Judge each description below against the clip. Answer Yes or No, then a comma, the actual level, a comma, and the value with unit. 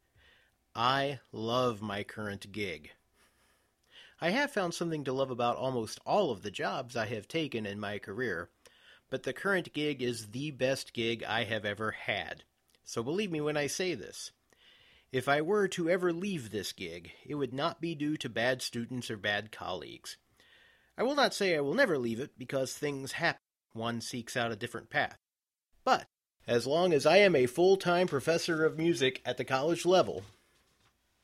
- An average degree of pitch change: No, wide, 5.9 semitones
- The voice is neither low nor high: No, low, 130 Hz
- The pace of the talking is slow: No, average, 185 wpm